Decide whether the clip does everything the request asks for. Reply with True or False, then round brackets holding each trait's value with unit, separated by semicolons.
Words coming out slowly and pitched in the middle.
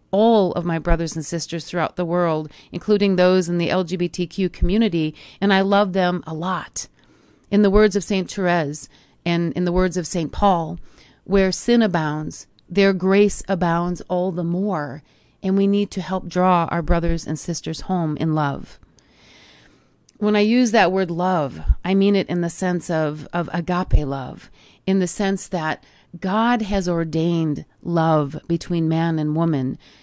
False (170 wpm; 175 Hz)